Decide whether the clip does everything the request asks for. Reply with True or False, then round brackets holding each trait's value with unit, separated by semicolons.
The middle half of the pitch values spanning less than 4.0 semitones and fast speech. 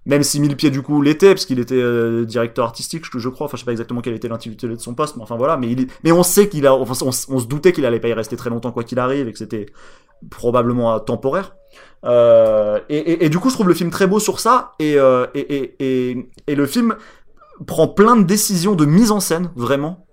False (5.6 semitones; 255 wpm)